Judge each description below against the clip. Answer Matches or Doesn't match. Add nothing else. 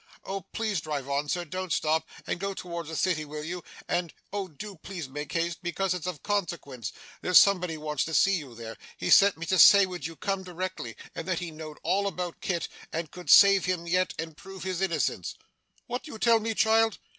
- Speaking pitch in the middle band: Matches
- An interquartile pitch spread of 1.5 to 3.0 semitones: Doesn't match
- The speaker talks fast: Matches